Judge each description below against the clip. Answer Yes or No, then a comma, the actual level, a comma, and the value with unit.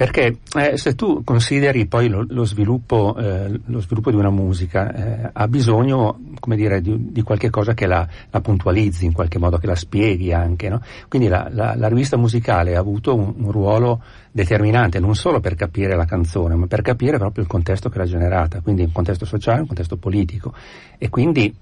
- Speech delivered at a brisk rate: Yes, fast, 195 wpm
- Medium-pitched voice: No, low, 105 Hz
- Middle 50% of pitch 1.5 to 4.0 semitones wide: Yes, average, 3.6 semitones